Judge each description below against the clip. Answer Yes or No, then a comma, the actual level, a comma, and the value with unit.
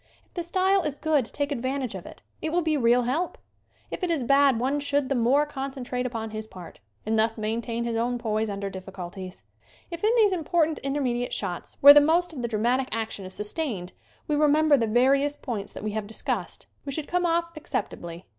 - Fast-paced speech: Yes, fast, 210 wpm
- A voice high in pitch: Yes, very high, 255 Hz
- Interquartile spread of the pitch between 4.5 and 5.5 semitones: Yes, average, 5.2 semitones